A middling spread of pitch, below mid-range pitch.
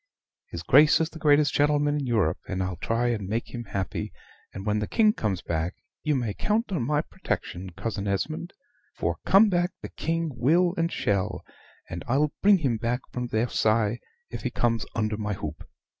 No: wide, 6.7 semitones; low, 120 Hz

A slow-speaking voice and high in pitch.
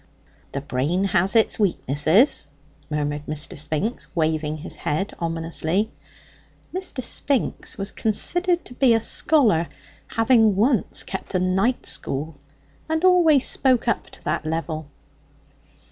Yes: slow, 125 wpm; high, 195 Hz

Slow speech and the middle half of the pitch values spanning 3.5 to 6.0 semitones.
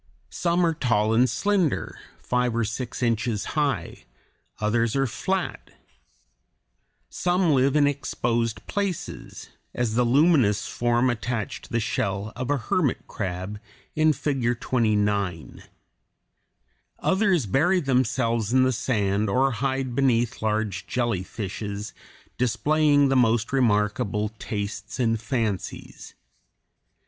Yes: slow, 115 wpm; average, 4.2 semitones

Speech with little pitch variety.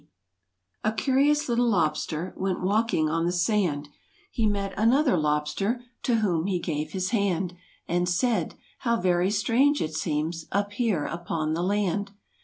No: average, 5.1 semitones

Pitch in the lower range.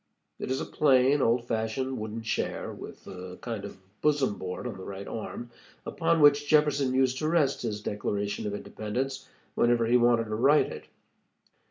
Yes: low, 120 Hz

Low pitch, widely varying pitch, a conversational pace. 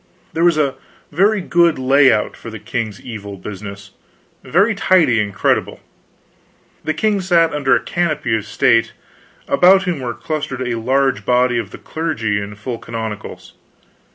Yes: low, 130 Hz; wide, 6.8 semitones; average, 155 wpm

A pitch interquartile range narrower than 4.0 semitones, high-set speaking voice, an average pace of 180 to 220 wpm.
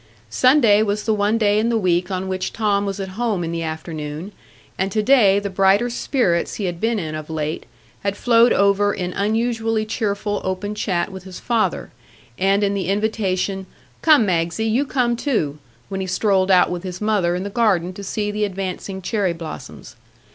Yes: average, 2.9 semitones; high, 200 Hz; average, 190 wpm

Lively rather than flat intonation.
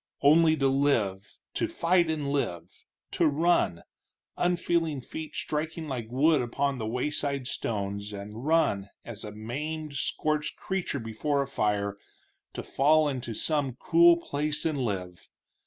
Yes: wide, 5.8 semitones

